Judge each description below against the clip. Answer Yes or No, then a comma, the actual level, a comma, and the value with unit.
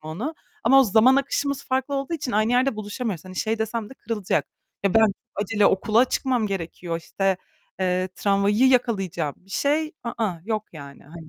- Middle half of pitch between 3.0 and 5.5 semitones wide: Yes, average, 5.2 semitones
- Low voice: No, high, 215 Hz